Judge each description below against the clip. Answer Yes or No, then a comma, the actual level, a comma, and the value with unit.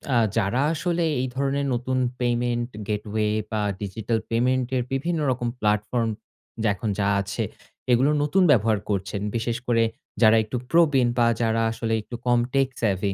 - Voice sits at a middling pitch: No, low, 120 Hz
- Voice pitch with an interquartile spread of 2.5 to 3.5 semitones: Yes, average, 3.1 semitones